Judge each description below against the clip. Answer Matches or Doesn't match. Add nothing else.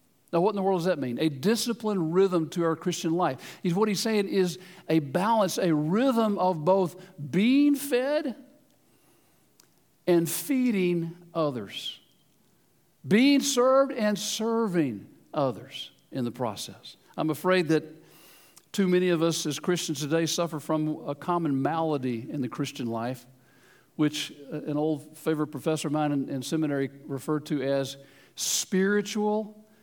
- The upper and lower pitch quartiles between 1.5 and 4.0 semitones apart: Doesn't match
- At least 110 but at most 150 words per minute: Matches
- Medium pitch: Matches